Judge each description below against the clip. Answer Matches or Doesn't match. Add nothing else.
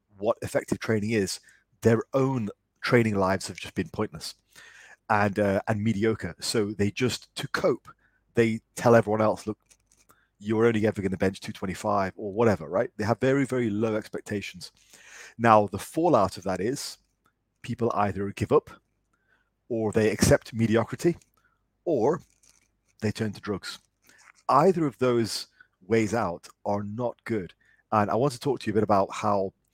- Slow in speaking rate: Doesn't match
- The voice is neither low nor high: Doesn't match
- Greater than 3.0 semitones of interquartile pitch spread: Doesn't match